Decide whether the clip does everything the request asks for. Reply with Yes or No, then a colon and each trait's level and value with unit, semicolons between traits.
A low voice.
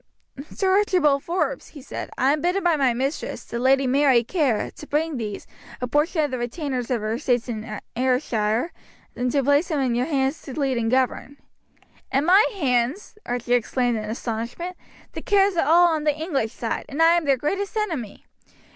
No: very high, 275 Hz